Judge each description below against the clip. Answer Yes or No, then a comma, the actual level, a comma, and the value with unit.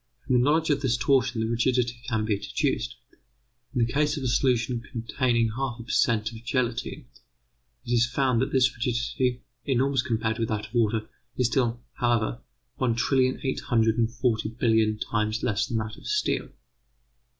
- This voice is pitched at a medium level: No, low, 120 Hz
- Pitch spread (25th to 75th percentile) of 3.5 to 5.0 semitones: No, narrow, 2.4 semitones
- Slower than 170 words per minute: No, average, 175 wpm